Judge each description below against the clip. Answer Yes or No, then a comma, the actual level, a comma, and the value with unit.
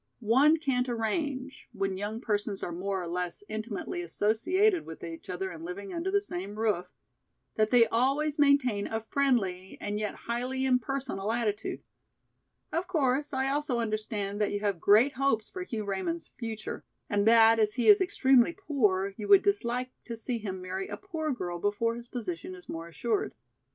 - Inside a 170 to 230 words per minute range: Yes, average, 175 wpm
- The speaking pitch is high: Yes, high, 225 Hz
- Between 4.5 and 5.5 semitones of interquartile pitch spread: Yes, average, 5.2 semitones